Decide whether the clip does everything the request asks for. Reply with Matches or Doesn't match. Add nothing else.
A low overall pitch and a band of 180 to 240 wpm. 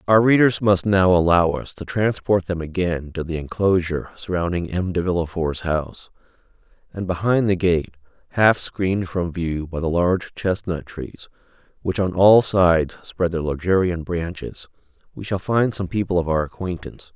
Doesn't match